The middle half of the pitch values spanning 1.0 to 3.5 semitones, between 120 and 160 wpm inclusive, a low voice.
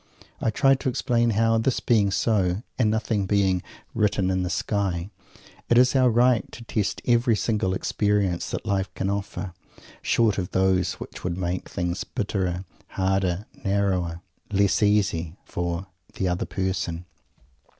Yes: average, 3.2 semitones; average, 150 wpm; low, 100 Hz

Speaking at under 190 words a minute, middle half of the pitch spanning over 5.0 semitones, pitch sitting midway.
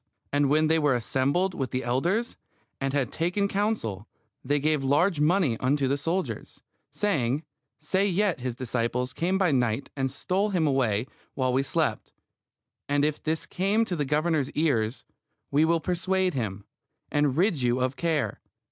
Yes: average, 165 wpm; wide, 5.4 semitones; medium, 145 Hz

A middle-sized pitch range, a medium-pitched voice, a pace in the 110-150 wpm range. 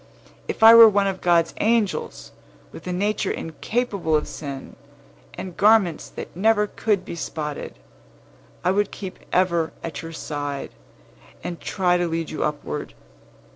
Yes: average, 4.3 semitones; medium, 180 Hz; average, 145 wpm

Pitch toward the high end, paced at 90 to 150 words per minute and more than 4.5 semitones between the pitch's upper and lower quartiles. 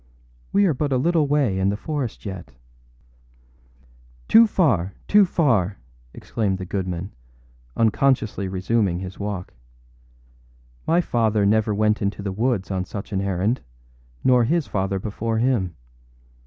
No: low, 105 Hz; slow, 135 wpm; average, 5.2 semitones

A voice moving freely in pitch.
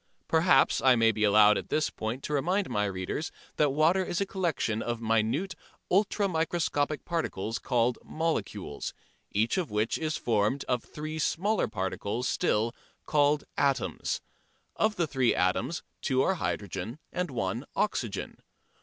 Yes: wide, 6.8 semitones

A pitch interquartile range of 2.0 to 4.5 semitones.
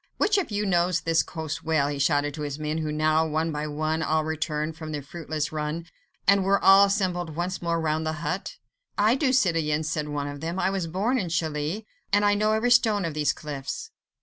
Yes: average, 3.9 semitones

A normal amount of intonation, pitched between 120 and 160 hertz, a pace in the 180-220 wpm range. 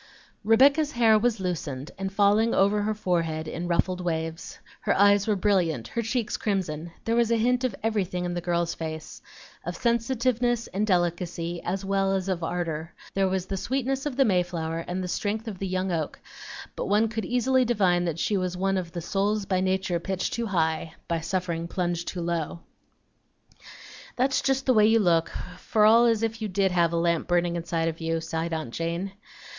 No: average, 4.2 semitones; medium, 185 Hz; average, 200 wpm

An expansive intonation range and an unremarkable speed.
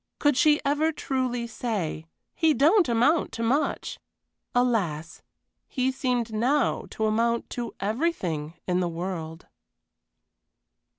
No: wide, 6.6 semitones; slow, 115 wpm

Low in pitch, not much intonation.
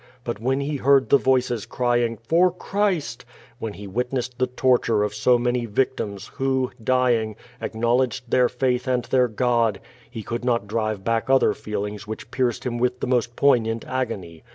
Yes: low, 120 Hz; narrow, 2.3 semitones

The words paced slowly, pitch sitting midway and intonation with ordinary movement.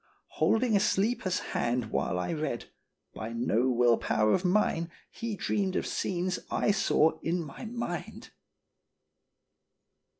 No: slow, 130 wpm; medium, 175 Hz; wide, 8.8 semitones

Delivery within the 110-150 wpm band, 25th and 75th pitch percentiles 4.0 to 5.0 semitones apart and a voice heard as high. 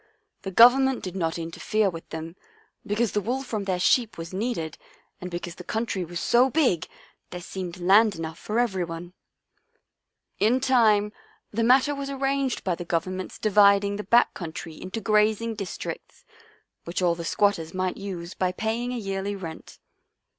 No: average, 165 wpm; average, 4.6 semitones; high, 200 Hz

